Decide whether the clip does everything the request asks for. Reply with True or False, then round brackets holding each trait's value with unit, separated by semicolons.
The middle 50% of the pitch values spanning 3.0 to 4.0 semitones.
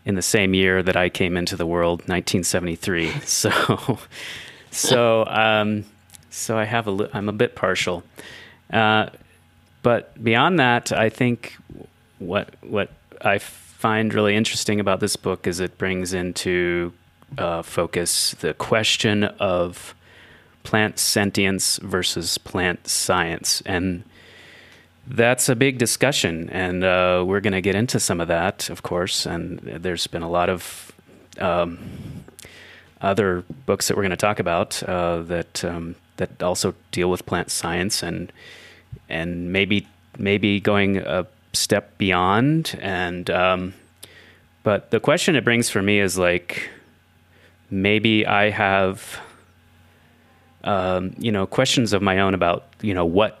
True (3.4 semitones)